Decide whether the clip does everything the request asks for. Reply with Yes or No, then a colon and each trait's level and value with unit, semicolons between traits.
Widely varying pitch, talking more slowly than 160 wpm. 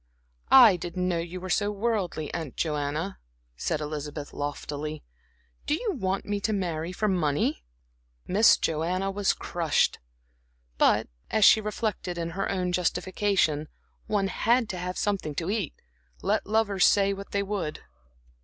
No: average, 4.4 semitones; average, 145 wpm